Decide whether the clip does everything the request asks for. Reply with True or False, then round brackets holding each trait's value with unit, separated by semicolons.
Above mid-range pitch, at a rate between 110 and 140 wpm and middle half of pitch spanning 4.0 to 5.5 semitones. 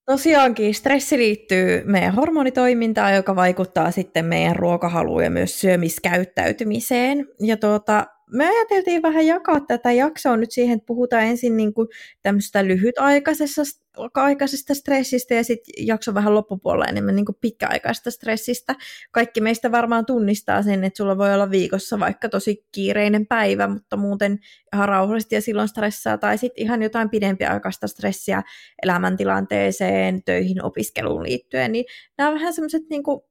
True (225 Hz; 135 wpm; 4.4 semitones)